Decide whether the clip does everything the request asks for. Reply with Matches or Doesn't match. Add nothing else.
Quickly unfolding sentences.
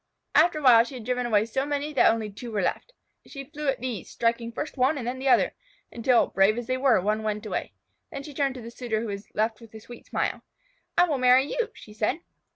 Matches